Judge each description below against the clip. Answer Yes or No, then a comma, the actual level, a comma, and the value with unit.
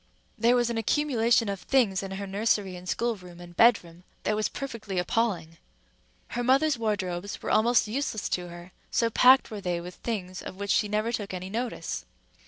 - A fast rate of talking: No, average, 185 wpm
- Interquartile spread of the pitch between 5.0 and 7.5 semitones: No, average, 4.3 semitones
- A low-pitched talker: No, high, 210 Hz